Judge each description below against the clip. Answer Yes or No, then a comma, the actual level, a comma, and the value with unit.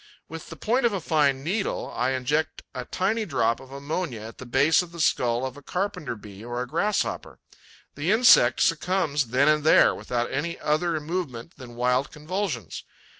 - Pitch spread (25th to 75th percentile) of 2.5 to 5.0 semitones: No, wide, 5.5 semitones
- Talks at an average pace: Yes, average, 180 wpm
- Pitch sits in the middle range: Yes, medium, 145 Hz